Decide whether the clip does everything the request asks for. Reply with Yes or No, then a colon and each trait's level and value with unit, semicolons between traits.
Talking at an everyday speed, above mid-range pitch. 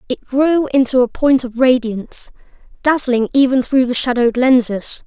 Yes: average, 155 wpm; very high, 255 Hz